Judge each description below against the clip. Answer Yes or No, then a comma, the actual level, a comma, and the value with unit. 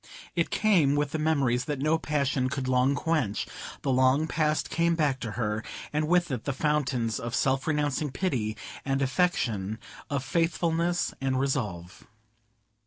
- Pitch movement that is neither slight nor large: Yes, average, 3.6 semitones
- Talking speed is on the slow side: No, average, 155 wpm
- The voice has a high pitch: No, medium, 140 Hz